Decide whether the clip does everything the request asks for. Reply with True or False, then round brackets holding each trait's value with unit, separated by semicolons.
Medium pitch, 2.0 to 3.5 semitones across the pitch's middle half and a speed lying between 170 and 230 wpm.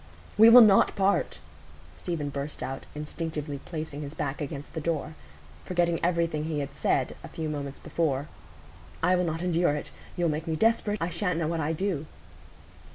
True (160 Hz; 2.9 semitones; 175 wpm)